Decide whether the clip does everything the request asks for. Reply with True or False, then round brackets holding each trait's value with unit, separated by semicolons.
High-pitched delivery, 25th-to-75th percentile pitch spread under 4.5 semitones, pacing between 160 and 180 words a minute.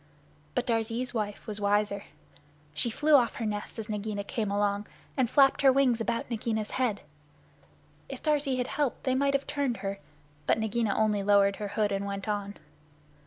True (220 Hz; 3.6 semitones; 175 wpm)